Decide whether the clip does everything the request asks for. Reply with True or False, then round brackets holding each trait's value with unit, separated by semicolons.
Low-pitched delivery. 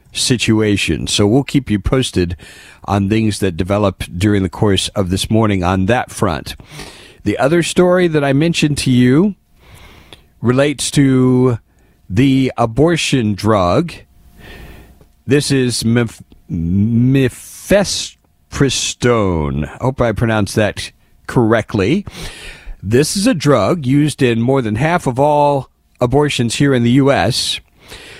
True (115 Hz)